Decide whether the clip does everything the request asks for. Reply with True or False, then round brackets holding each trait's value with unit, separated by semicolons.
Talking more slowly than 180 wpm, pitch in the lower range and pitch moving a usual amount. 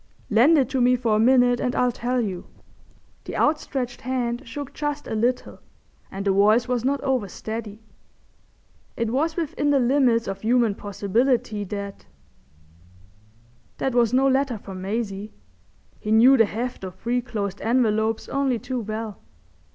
False (150 wpm; 230 Hz; 4.0 semitones)